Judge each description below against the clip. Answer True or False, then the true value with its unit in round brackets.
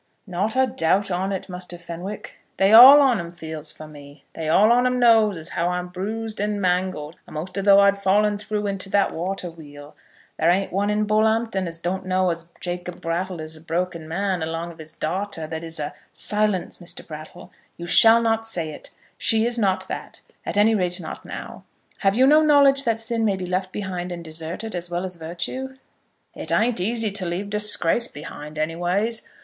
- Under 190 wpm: False (205 wpm)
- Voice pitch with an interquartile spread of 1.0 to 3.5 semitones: False (4.0 semitones)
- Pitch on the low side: False (185 Hz)